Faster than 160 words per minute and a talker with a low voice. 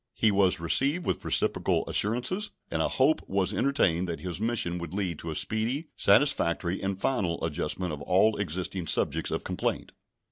Yes: average, 170 wpm; very low, 95 Hz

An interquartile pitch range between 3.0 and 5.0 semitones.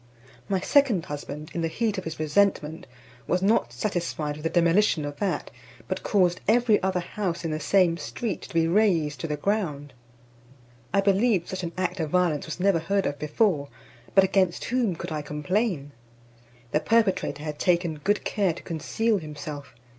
Yes: average, 4.6 semitones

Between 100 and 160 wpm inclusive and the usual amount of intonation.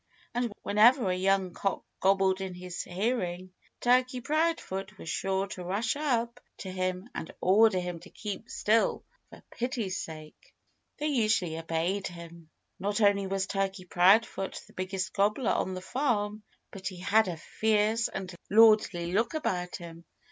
Yes: average, 155 wpm; average, 3.4 semitones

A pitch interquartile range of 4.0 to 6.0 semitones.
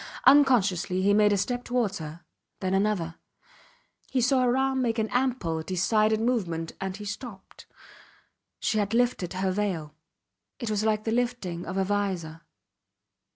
Yes: average, 4.6 semitones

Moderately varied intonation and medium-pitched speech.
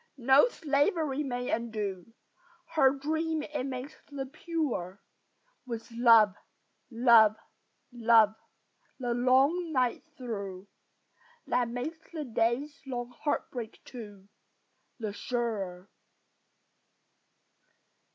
No: average, 3.9 semitones; high, 245 Hz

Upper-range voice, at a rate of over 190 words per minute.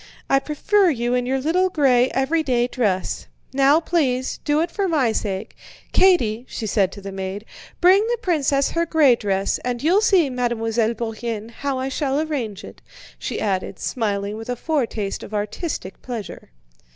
No: very high, 250 Hz; average, 165 wpm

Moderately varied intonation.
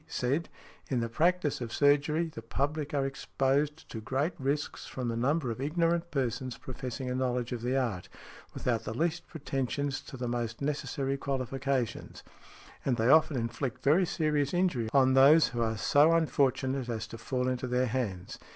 Yes: average, 3.2 semitones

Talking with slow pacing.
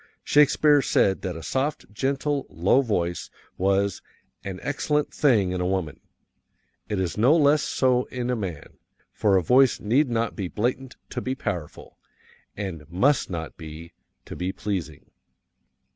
No: average, 145 wpm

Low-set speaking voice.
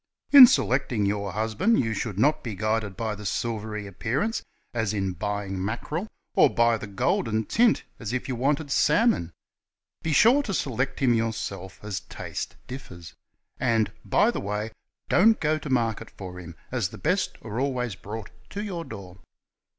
Yes: low, 115 Hz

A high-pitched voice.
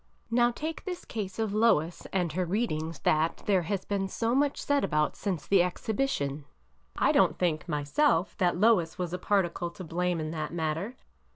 No: medium, 180 Hz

